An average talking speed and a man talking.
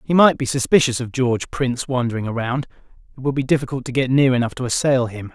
No: fast, 225 wpm; male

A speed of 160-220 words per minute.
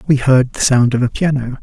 No: fast, 260 wpm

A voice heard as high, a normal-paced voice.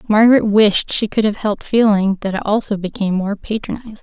Yes: high, 210 Hz; average, 195 wpm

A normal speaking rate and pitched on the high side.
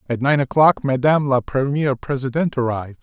No: average, 160 wpm; low, 135 Hz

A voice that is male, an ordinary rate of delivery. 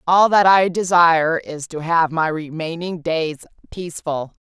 No: female; average, 150 wpm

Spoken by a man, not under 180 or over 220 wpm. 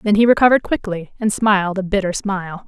No: female; average, 200 wpm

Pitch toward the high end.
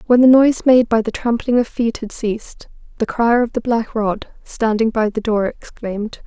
Yes: high, 230 Hz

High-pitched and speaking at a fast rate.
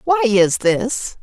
No: high, 235 Hz; average, 145 wpm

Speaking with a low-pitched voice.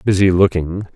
Yes: very low, 95 Hz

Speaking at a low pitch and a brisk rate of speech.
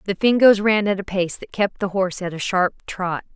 No: high, 195 Hz; fast, 250 wpm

